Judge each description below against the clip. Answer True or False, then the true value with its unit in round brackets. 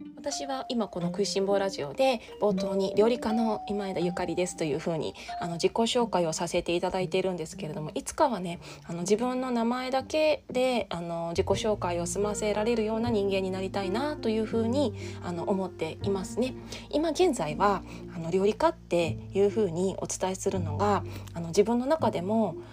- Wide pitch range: False (4.6 semitones)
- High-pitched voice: True (195 Hz)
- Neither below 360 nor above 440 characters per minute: True (380 characters per minute)